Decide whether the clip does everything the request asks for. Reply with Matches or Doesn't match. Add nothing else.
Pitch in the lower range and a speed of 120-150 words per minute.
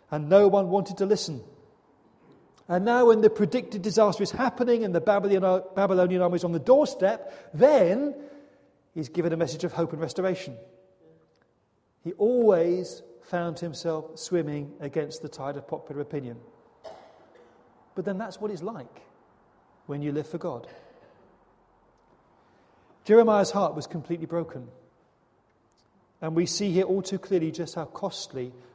Doesn't match